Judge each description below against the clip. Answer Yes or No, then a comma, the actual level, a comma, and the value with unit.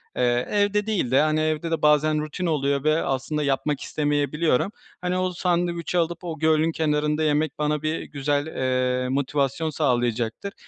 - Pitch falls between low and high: Yes, medium, 150 Hz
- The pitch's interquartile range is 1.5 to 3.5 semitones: Yes, average, 2.9 semitones